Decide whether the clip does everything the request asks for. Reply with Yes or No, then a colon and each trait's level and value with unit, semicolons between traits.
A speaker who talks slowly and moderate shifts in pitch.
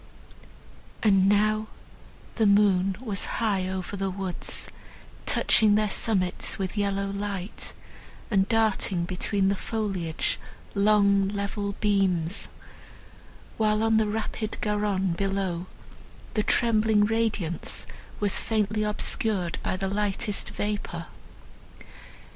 No: slow, 105 wpm; narrow, 1.8 semitones